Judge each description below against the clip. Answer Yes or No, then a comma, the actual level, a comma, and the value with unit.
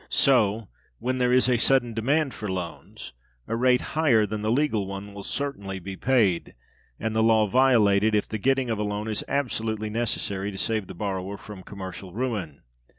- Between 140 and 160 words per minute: No, average, 185 wpm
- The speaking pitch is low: Yes, low, 110 Hz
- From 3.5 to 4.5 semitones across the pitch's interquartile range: Yes, average, 3.9 semitones